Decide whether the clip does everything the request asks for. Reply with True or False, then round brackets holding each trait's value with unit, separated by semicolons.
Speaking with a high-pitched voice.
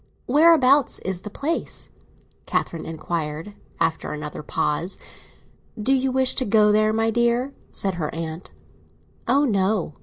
True (210 Hz)